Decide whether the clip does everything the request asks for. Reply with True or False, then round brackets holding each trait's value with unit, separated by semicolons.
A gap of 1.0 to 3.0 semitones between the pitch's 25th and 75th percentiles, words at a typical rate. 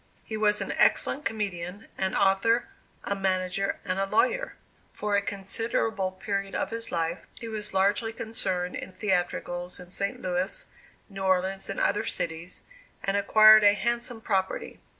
True (2.6 semitones; 150 wpm)